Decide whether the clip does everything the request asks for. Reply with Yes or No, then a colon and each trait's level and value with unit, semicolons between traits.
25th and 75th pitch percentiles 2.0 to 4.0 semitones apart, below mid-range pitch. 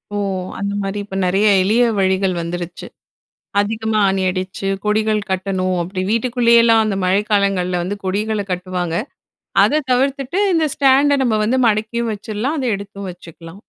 No: average, 3.7 semitones; high, 205 Hz